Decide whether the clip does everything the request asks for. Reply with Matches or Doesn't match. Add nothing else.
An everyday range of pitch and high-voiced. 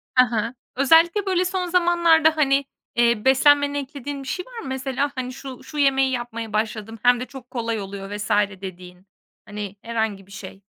Matches